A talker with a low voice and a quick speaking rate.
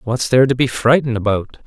Yes: low, 120 Hz; fast, 215 wpm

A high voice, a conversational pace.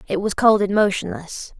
Yes: high, 205 Hz; average, 190 wpm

